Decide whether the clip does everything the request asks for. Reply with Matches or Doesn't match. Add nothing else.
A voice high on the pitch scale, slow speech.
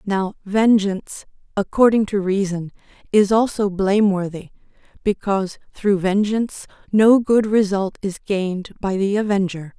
Matches